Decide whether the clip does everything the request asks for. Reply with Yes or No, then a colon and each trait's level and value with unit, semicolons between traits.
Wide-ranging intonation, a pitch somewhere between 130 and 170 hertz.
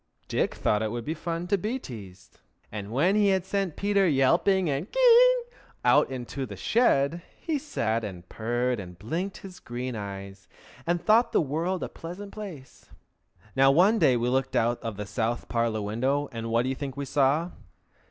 Yes: wide, 8.3 semitones; low, 135 Hz